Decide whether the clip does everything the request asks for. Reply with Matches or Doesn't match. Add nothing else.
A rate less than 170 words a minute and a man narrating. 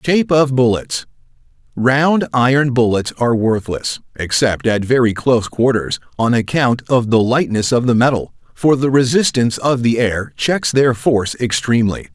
Matches